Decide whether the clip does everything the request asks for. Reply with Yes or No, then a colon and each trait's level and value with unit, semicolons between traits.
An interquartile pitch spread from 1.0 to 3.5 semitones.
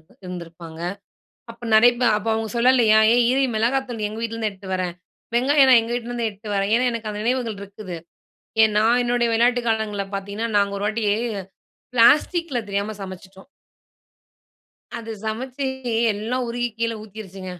Yes: average, 3.1 semitones